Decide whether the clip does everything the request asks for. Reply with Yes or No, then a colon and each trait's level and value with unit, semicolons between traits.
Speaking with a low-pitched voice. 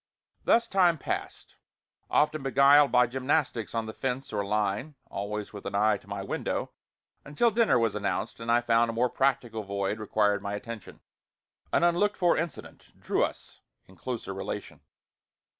Yes: low, 115 Hz